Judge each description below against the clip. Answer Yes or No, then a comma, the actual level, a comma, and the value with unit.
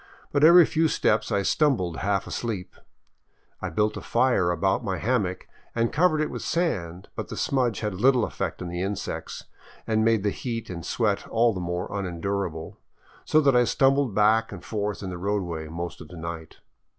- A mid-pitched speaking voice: No, low, 105 Hz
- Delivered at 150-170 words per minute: No, average, 185 wpm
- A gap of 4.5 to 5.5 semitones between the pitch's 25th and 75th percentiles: Yes, average, 5.2 semitones